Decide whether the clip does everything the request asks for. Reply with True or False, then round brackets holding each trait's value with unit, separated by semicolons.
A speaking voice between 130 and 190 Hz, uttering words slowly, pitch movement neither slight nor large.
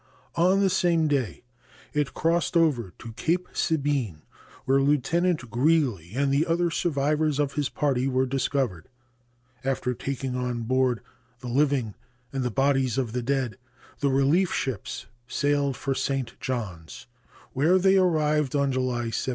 False (135 Hz; 145 wpm; 3.3 semitones)